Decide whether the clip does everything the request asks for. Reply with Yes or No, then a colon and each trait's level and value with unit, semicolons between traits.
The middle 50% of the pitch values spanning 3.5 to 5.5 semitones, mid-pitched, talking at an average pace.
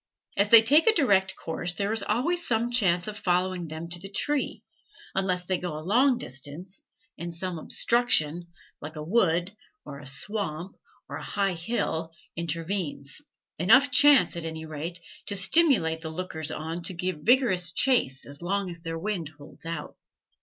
Yes: average, 4.5 semitones; medium, 180 Hz; average, 170 wpm